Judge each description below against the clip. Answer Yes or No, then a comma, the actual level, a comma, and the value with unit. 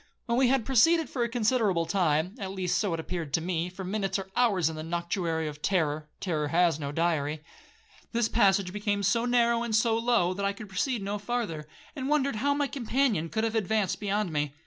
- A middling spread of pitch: No, wide, 5.7 semitones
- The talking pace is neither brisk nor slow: No, fast, 210 wpm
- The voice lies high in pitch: Yes, high, 200 Hz